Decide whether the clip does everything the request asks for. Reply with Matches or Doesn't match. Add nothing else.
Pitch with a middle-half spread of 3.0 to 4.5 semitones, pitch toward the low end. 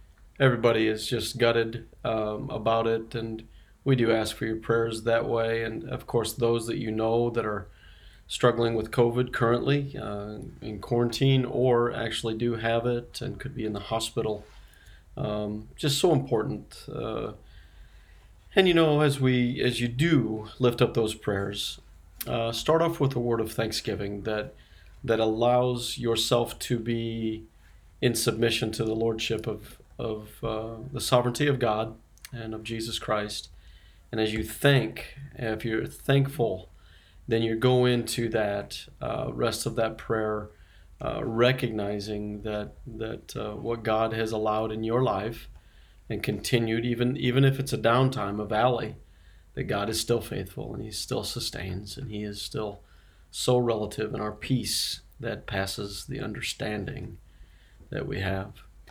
Doesn't match